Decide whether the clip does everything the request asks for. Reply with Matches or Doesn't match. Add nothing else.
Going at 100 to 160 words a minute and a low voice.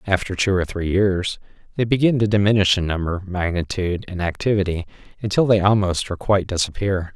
Doesn't match